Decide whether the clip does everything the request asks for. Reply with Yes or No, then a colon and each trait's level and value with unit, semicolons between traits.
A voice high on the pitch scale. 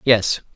No: low, 110 Hz